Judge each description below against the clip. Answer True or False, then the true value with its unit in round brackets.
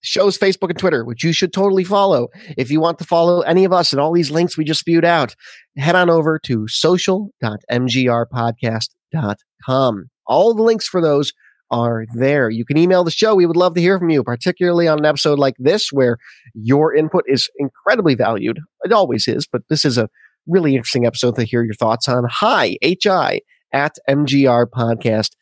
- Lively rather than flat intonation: True (6.5 semitones)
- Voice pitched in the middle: True (150 Hz)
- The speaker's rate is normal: True (190 wpm)